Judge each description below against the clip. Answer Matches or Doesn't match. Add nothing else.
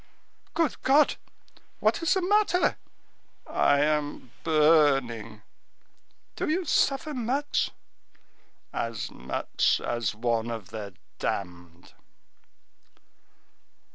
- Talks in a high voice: Doesn't match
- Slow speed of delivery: Matches